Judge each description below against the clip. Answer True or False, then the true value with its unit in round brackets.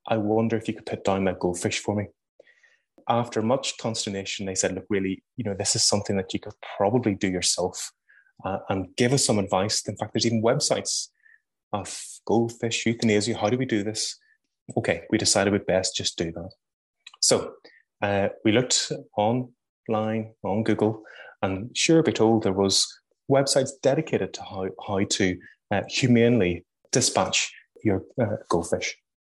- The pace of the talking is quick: False (165 wpm)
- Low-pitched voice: True (110 Hz)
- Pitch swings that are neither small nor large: True (3.2 semitones)